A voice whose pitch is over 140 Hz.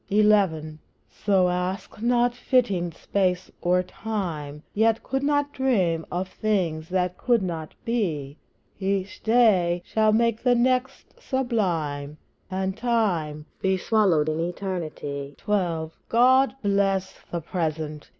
Yes: high, 190 Hz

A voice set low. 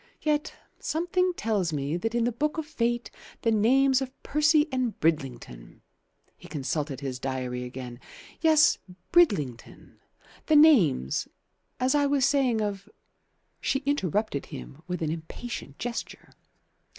No: high, 225 Hz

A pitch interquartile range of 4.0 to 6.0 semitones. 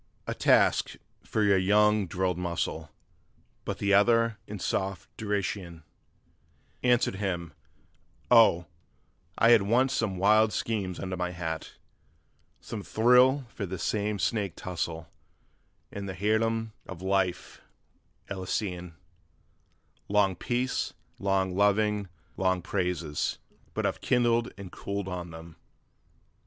No: average, 3.2 semitones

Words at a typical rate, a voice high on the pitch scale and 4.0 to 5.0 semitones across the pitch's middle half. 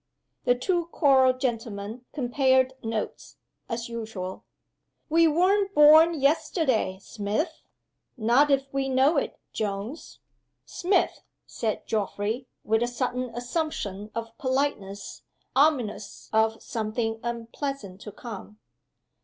No: slow, 105 wpm; high, 245 Hz; average, 4.5 semitones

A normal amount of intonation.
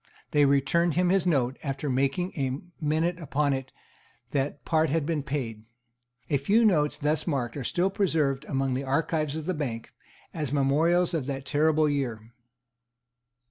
Yes: average, 3.2 semitones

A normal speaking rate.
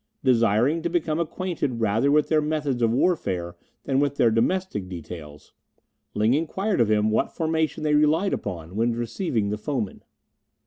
Yes: average, 160 wpm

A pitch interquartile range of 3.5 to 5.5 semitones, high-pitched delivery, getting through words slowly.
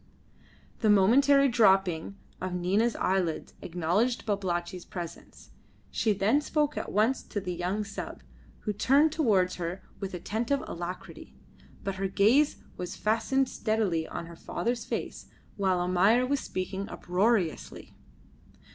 Yes: average, 4.6 semitones; high, 200 Hz; slow, 130 wpm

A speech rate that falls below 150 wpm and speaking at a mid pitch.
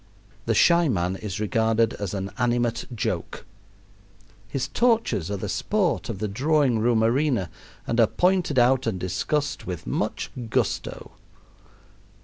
No: slow, 135 wpm; low, 115 Hz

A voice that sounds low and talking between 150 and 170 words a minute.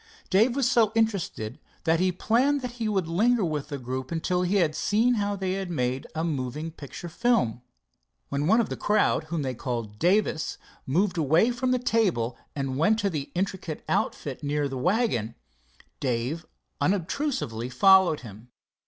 No: medium, 170 Hz; average, 165 wpm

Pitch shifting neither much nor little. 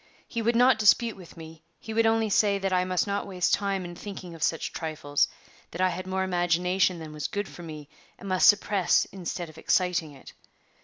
Yes: average, 3.1 semitones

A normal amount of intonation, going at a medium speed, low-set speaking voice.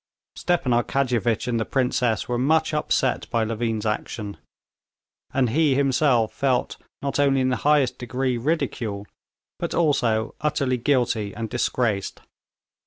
No: average, 3.2 semitones; slow, 130 wpm; low, 125 Hz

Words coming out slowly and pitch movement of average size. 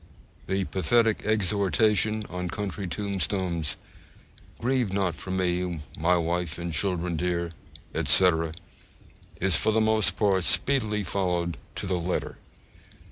Yes: slow, 120 wpm; average, 3.1 semitones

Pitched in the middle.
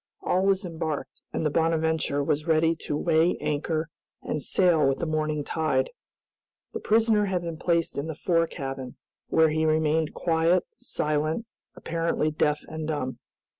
Yes: medium, 160 Hz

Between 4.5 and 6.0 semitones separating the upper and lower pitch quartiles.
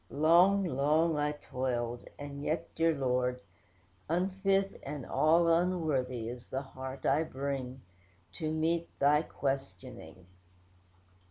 No: average, 4.1 semitones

